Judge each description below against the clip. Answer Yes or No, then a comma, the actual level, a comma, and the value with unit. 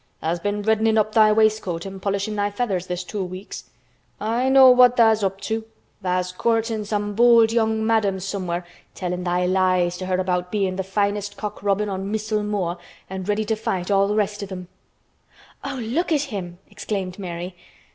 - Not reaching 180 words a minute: No, average, 185 wpm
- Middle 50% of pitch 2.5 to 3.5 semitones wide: Yes, average, 2.9 semitones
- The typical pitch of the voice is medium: No, high, 205 Hz